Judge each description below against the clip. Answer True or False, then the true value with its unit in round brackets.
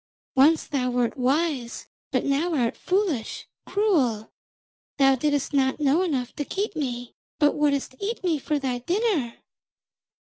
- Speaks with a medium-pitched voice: False (280 Hz)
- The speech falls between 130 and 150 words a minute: True (140 wpm)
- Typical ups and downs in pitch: True (4.6 semitones)